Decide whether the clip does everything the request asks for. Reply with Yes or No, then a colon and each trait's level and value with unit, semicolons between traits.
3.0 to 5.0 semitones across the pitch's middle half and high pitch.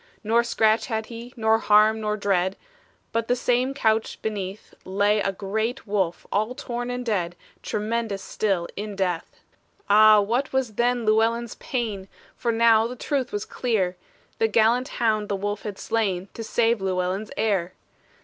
No: narrow, 2.6 semitones; high, 220 Hz